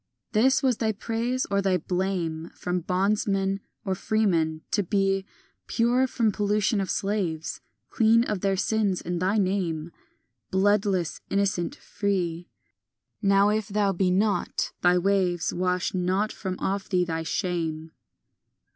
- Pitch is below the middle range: No, high, 195 Hz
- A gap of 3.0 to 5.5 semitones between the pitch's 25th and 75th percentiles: No, narrow, 2.6 semitones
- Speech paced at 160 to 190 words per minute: No, slow, 135 wpm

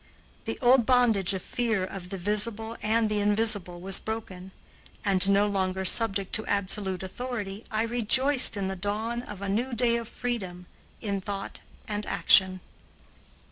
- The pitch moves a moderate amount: Yes, average, 3.1 semitones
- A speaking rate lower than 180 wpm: Yes, average, 155 wpm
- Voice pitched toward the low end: No, high, 205 Hz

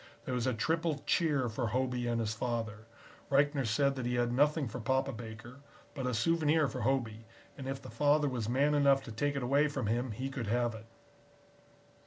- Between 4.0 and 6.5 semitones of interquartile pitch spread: No, average, 3.3 semitones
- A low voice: Yes, low, 130 Hz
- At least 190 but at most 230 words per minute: Yes, fast, 205 wpm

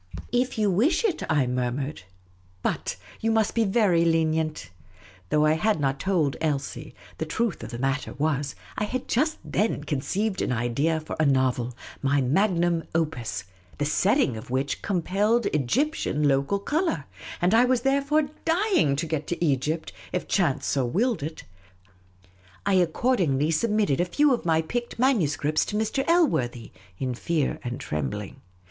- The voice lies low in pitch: No, medium, 160 Hz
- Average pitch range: No, wide, 8.1 semitones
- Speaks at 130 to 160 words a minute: No, average, 170 wpm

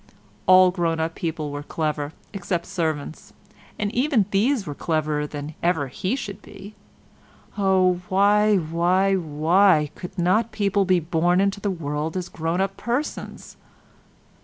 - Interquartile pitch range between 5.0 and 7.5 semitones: No, average, 3.8 semitones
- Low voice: No, medium, 180 Hz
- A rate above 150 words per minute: No, slow, 135 wpm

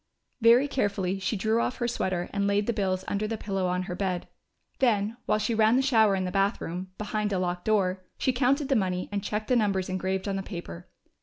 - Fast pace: Yes, fast, 225 wpm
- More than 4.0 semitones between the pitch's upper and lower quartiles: No, average, 2.9 semitones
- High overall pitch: Yes, high, 200 Hz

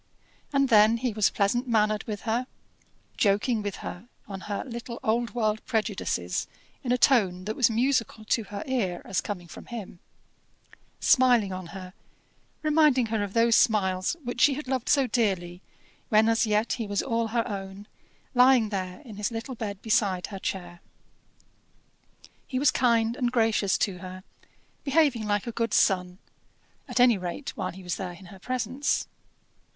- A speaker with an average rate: Yes, average, 165 wpm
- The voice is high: Yes, high, 220 Hz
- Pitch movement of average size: Yes, average, 3.8 semitones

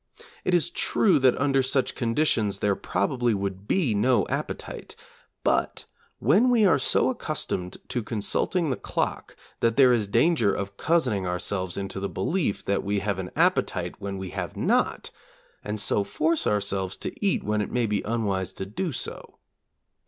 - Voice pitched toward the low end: Yes, low, 105 Hz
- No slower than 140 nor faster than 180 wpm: Yes, average, 165 wpm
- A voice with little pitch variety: No, wide, 5.5 semitones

